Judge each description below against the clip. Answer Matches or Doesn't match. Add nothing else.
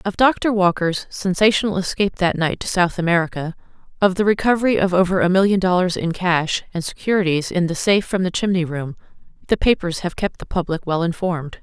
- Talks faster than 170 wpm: Matches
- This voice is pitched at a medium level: Matches